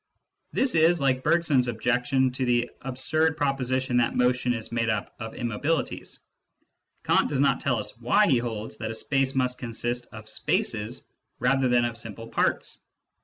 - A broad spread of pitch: No, narrow, 2.5 semitones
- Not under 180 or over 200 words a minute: No, average, 165 wpm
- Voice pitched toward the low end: Yes, low, 125 Hz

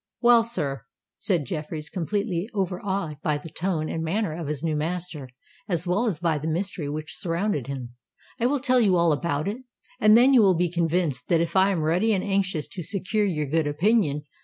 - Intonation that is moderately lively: Yes, average, 4.5 semitones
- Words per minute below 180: No, average, 200 wpm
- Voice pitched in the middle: Yes, medium, 175 Hz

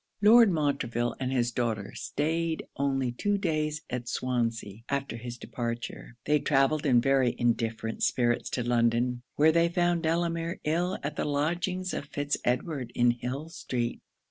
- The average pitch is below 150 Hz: Yes, low, 135 Hz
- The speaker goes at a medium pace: Yes, average, 150 wpm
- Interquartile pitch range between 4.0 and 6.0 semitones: Yes, average, 5.0 semitones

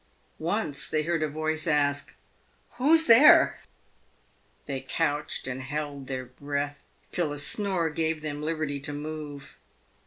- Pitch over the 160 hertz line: No, medium, 150 Hz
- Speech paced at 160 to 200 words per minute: No, average, 145 wpm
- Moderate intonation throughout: No, narrow, 2.1 semitones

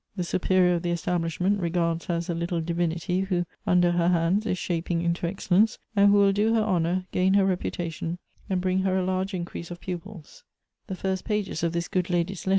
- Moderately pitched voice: Yes, medium, 180 Hz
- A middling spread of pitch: No, narrow, 1.8 semitones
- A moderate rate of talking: No, fast, 220 wpm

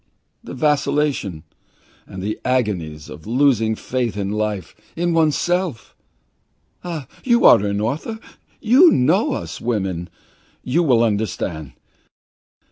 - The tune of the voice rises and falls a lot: Yes, wide, 7.6 semitones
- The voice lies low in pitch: Yes, low, 120 Hz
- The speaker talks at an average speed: No, slow, 115 wpm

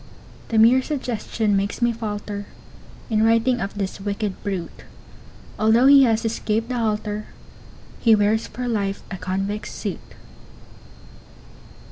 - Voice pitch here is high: Yes, high, 215 Hz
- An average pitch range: No, narrow, 2.2 semitones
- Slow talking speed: Yes, slow, 125 wpm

